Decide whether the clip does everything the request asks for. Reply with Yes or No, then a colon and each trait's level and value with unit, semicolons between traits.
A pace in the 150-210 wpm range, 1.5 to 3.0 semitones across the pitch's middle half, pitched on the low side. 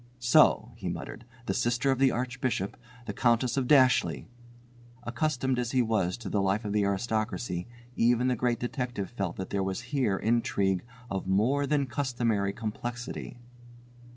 No: average, 155 wpm; average, 3.7 semitones; low, 120 Hz